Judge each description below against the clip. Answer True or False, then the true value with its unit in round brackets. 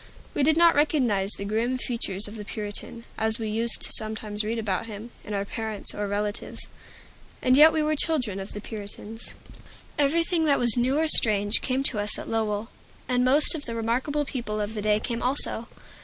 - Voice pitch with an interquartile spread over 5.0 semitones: False (4.0 semitones)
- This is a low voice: False (225 Hz)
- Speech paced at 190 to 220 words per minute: True (200 wpm)